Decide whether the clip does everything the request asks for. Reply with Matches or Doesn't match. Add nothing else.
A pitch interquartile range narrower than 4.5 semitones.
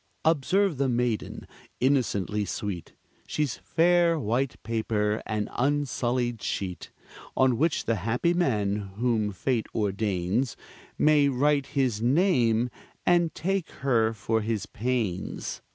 Doesn't match